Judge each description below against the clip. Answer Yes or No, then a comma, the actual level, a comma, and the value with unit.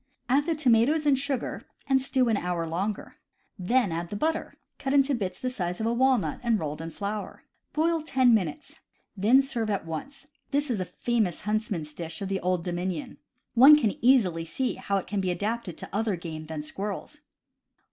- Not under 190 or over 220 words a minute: Yes, average, 195 wpm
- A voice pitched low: No, high, 215 Hz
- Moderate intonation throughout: No, wide, 6.6 semitones